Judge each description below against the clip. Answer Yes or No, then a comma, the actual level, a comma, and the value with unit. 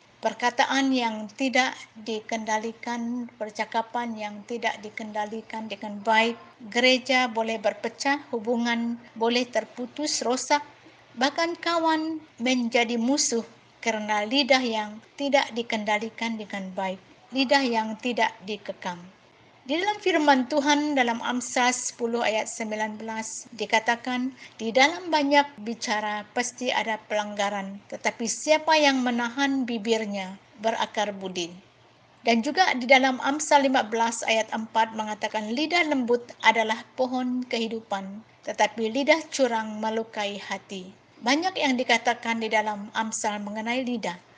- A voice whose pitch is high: Yes, high, 230 Hz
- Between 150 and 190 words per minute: No, average, 110 wpm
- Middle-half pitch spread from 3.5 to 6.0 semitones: No, average, 3.1 semitones